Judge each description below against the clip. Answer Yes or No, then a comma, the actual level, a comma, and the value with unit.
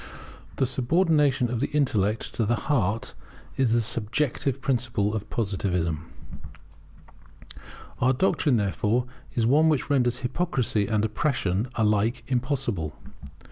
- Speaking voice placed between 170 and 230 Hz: No, low, 120 Hz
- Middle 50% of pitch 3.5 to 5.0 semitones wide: Yes, average, 4.2 semitones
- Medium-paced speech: No, slow, 115 wpm